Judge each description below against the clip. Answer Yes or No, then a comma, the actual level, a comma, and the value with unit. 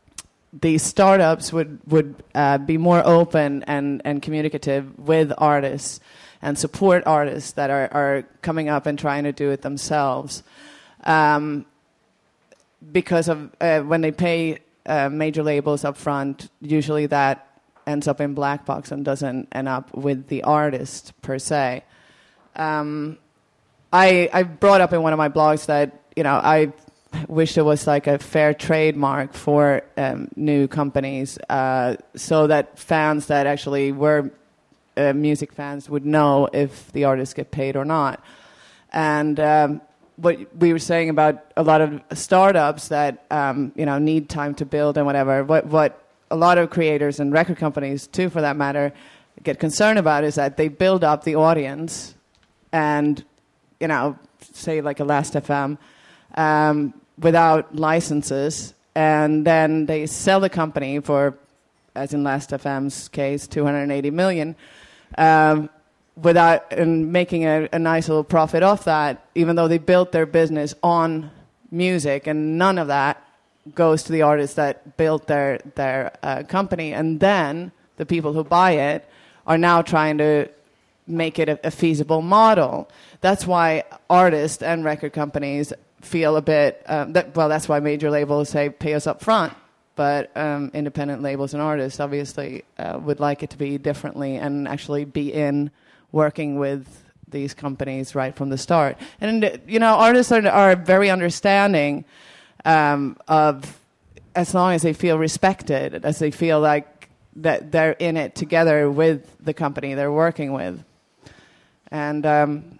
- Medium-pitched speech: Yes, medium, 150 Hz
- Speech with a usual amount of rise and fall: No, narrow, 2.2 semitones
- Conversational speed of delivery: Yes, average, 160 wpm